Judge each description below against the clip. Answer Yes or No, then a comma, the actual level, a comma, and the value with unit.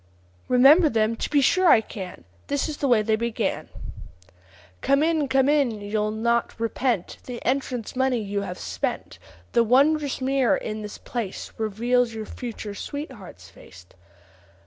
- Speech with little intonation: No, average, 4.1 semitones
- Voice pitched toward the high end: Yes, high, 235 Hz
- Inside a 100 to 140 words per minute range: No, average, 150 wpm